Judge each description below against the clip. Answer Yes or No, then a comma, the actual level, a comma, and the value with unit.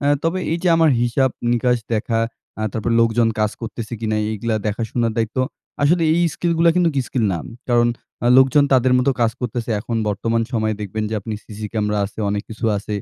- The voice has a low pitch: Yes, low, 115 Hz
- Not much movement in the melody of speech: No, average, 3.2 semitones